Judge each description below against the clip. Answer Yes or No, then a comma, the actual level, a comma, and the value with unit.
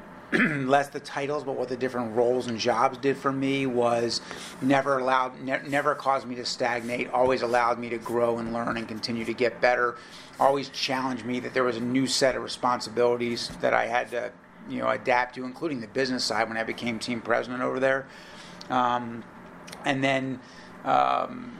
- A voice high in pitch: No, low, 125 Hz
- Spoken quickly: No, average, 190 wpm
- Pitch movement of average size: No, narrow, 2.1 semitones